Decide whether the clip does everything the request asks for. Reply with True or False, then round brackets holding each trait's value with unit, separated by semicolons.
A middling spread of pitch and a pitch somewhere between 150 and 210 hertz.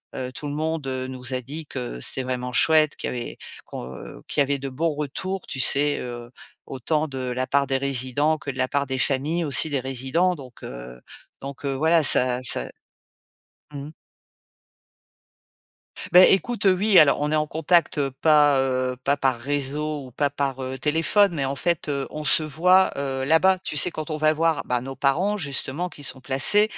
False (3.1 semitones; 140 Hz)